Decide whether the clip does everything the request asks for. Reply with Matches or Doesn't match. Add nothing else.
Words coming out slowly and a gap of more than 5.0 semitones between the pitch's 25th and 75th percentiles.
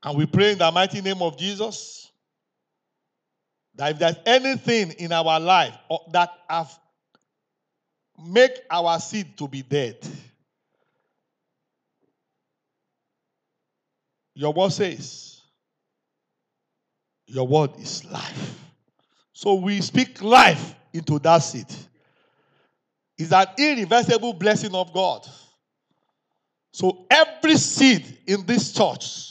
Matches